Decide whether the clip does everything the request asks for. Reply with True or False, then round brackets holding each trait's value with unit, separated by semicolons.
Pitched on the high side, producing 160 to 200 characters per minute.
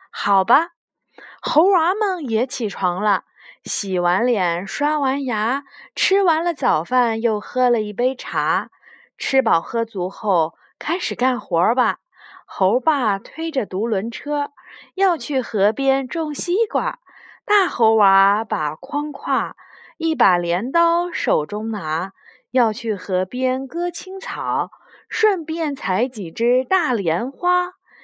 True (255 Hz; 165 characters per minute)